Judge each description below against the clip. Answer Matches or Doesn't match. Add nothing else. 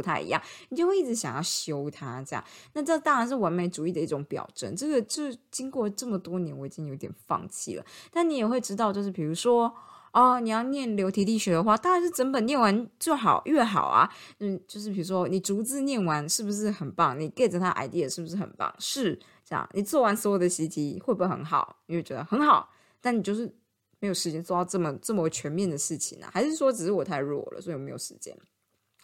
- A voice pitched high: Matches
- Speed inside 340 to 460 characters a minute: Matches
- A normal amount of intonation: Doesn't match